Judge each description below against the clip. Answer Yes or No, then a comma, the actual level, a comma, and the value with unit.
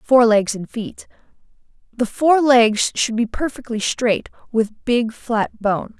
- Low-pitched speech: No, high, 210 Hz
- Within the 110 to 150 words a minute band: Yes, average, 140 wpm